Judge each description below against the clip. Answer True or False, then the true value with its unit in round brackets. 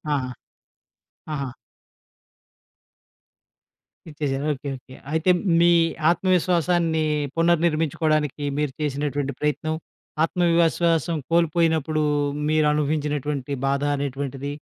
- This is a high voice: False (155 Hz)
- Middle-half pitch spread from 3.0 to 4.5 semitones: False (2.6 semitones)